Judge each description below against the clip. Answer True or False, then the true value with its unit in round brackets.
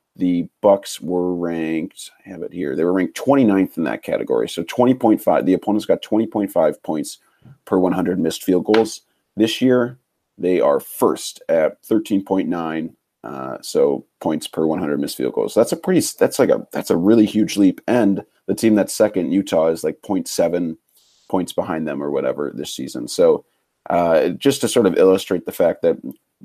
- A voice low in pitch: True (105 Hz)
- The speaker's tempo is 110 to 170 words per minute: False (180 wpm)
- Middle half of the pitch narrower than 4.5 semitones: False (5.6 semitones)